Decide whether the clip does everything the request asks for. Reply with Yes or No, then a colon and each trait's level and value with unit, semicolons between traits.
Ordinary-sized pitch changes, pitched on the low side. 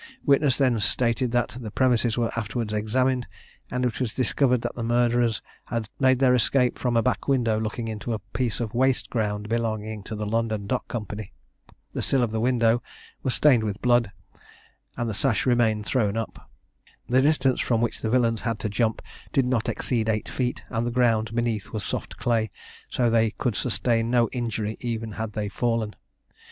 No: narrow, 2.2 semitones; low, 115 Hz